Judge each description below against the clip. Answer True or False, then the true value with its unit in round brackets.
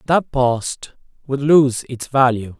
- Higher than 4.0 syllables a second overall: False (3.4 syllables/s)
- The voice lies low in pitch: True (130 Hz)